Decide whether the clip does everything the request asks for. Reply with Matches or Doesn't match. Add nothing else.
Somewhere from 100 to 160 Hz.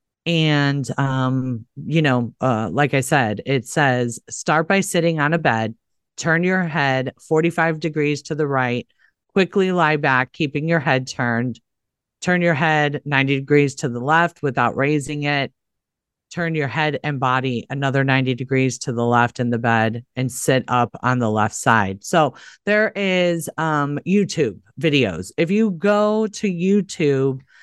Matches